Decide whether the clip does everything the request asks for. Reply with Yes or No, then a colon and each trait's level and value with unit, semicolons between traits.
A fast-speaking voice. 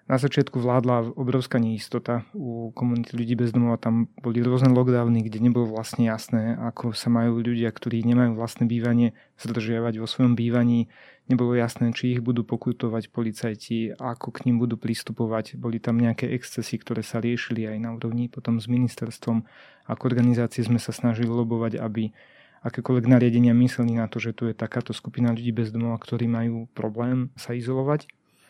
Yes: fast, 170 wpm